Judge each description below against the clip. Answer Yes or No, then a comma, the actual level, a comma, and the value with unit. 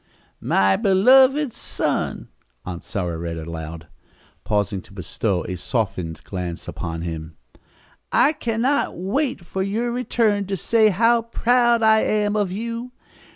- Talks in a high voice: Yes, high, 195 Hz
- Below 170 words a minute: Yes, slow, 135 wpm